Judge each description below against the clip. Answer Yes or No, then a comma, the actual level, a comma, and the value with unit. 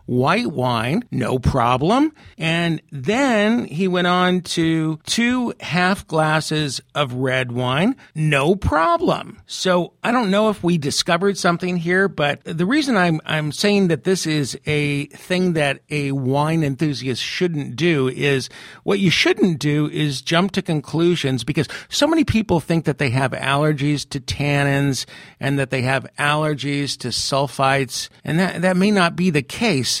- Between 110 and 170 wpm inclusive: Yes, average, 160 wpm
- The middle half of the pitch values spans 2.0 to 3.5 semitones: No, average, 4.6 semitones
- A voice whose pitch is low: No, medium, 155 Hz